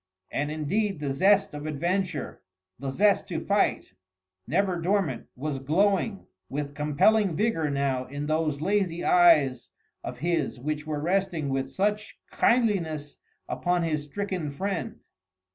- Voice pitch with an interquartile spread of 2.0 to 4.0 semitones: No, average, 5.0 semitones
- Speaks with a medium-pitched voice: Yes, medium, 160 Hz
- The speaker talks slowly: Yes, slow, 130 wpm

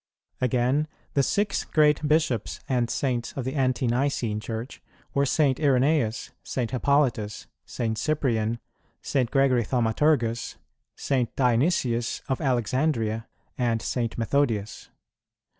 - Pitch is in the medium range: No, low, 125 Hz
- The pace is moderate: No, slow, 115 wpm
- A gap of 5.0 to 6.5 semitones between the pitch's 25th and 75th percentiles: No, average, 3.3 semitones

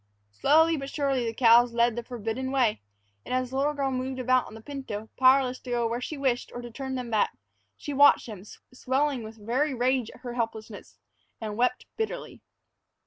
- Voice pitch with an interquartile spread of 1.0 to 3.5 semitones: Yes, narrow, 2.6 semitones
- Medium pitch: No, very high, 250 Hz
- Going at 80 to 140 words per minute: No, average, 195 wpm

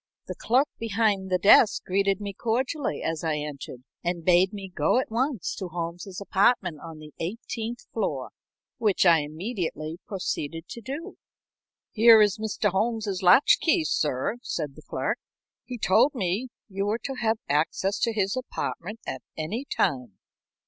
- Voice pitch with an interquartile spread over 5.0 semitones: Yes, wide, 5.4 semitones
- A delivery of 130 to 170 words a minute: Yes, average, 155 wpm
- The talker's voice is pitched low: No, high, 195 Hz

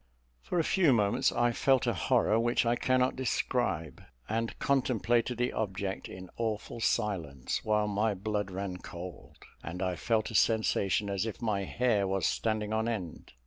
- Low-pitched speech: Yes, low, 110 Hz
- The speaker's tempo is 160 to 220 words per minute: Yes, average, 165 wpm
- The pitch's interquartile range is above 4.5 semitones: No, average, 3.4 semitones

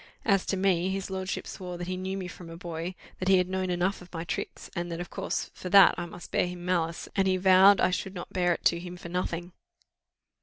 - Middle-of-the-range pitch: Yes, medium, 180 Hz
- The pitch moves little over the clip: Yes, narrow, 1.3 semitones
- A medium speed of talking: No, fast, 255 wpm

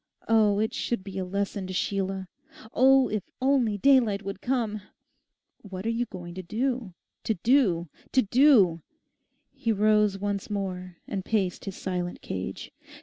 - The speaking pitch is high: Yes, high, 205 Hz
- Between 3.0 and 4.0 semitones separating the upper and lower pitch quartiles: Yes, average, 3.5 semitones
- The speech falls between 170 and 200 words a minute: No, average, 145 wpm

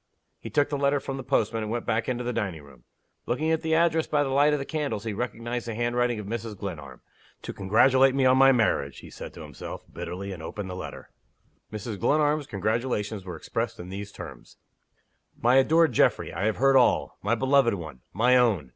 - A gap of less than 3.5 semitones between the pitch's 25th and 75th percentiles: No, average, 5.2 semitones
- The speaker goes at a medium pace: No, fast, 210 wpm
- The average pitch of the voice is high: No, low, 120 Hz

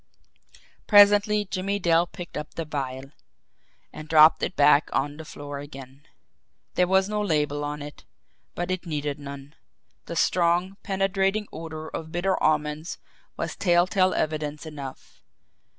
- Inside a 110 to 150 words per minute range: Yes, slow, 135 wpm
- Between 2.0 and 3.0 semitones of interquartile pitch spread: No, average, 4.1 semitones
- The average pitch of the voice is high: No, medium, 160 Hz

